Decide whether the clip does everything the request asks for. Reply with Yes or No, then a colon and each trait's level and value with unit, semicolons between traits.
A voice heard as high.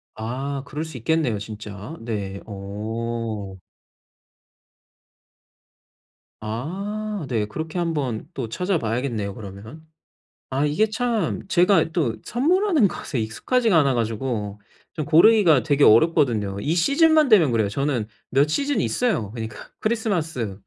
No: medium, 140 Hz